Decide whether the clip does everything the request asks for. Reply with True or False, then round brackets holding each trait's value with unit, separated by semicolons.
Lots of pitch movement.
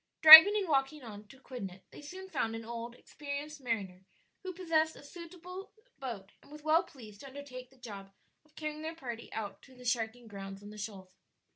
True (5.8 semitones)